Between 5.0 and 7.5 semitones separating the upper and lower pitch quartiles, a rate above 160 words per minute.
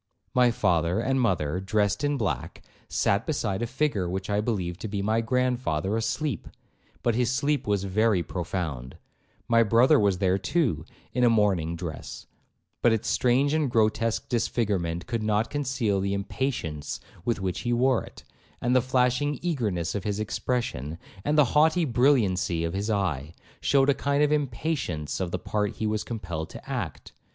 Yes: average, 5.3 semitones; average, 170 wpm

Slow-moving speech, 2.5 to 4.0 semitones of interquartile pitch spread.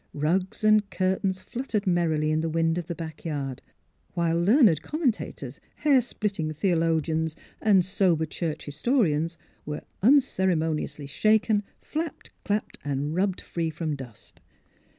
No: slow, 130 wpm; average, 4.7 semitones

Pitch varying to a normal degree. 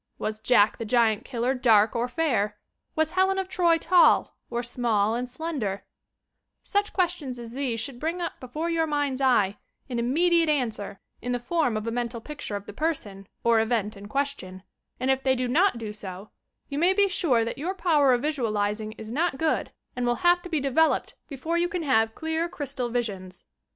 No: wide, 6.3 semitones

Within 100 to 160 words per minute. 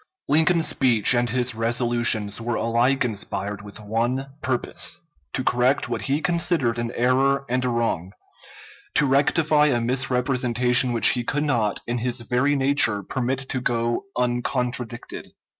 Yes: average, 140 wpm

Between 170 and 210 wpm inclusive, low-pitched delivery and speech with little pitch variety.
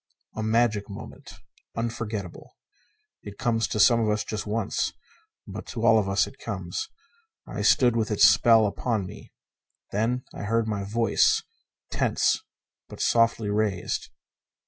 No: average, 145 wpm; low, 110 Hz; narrow, 2.0 semitones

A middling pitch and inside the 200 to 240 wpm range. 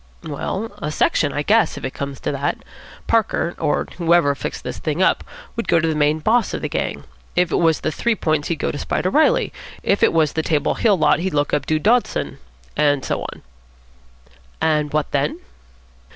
Yes: medium, 155 Hz; fast, 205 wpm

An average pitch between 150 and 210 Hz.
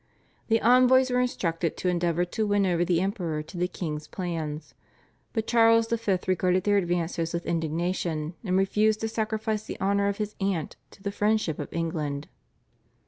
Yes: medium, 185 Hz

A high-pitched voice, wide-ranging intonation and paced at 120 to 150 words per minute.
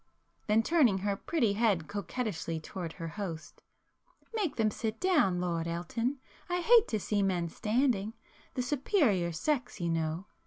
Yes: high, 205 Hz; wide, 6.6 semitones; average, 140 wpm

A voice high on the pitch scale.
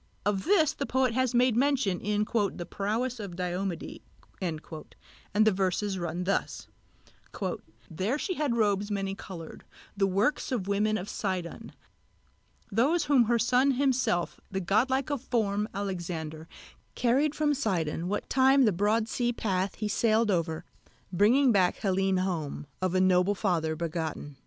Yes: high, 205 Hz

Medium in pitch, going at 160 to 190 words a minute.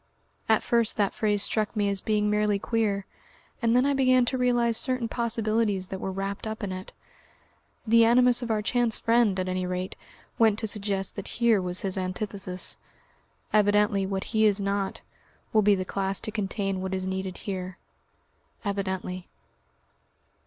No: high, 205 Hz; average, 165 wpm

